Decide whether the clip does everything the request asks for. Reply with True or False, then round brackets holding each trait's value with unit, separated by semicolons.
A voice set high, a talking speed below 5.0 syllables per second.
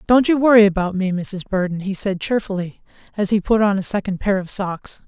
False (200 Hz; 5.5 syllables/s)